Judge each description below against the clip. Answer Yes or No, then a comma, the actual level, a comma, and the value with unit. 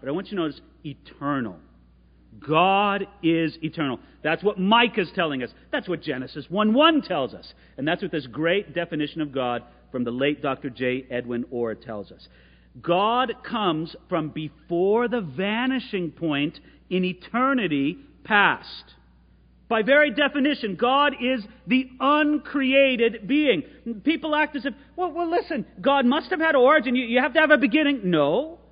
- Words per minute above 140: Yes, average, 160 wpm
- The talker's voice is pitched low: No, medium, 185 Hz